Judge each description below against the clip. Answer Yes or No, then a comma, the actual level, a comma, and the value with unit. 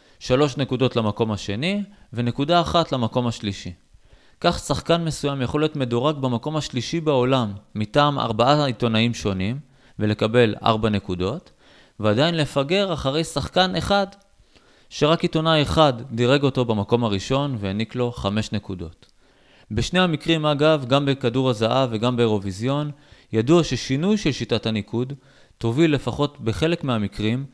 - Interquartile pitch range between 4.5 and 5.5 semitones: Yes, average, 5.0 semitones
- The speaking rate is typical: Yes, average, 125 wpm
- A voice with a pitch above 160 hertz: No, low, 130 Hz